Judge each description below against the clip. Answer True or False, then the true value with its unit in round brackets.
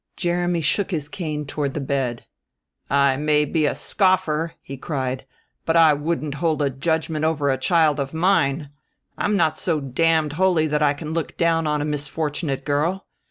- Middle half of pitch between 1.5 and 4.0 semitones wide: True (2.5 semitones)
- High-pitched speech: False (150 Hz)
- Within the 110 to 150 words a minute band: False (175 wpm)